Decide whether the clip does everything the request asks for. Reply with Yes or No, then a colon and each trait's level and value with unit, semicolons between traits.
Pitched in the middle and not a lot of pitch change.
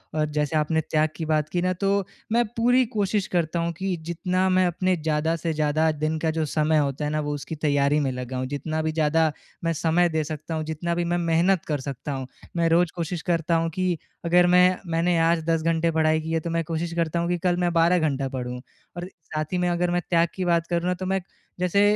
Yes: medium, 165 Hz; narrow, 2.3 semitones